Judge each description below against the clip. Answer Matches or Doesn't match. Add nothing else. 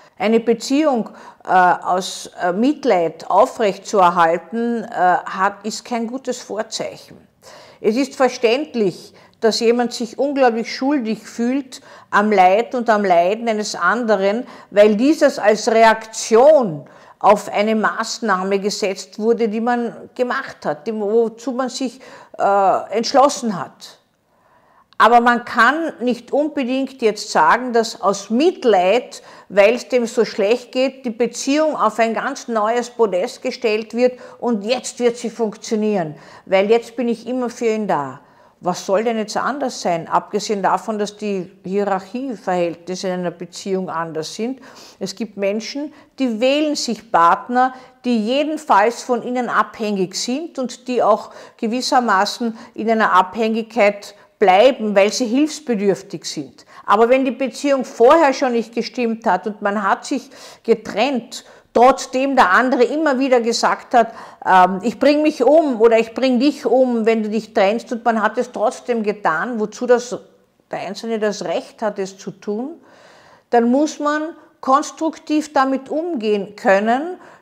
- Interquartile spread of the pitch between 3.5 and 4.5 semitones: Matches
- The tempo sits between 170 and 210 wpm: Doesn't match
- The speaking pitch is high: Matches